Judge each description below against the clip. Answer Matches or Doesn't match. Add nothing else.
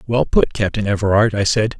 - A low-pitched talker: Matches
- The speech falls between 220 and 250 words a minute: Doesn't match